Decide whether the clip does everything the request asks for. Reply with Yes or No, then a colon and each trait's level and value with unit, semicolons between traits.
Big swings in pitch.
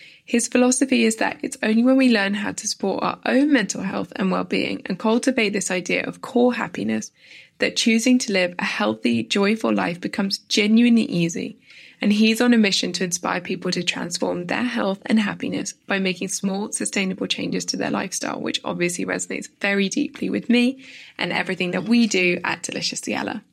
No: average, 4.2 semitones